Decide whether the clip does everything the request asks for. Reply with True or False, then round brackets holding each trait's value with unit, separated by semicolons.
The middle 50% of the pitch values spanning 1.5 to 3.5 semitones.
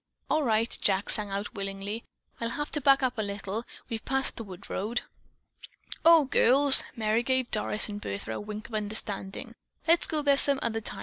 False (4.6 semitones)